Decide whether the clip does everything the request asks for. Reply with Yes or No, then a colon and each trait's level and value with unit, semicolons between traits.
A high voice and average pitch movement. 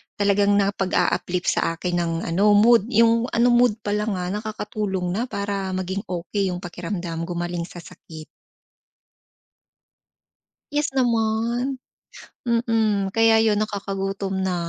Yes: high, 200 Hz; average, 3.6 semitones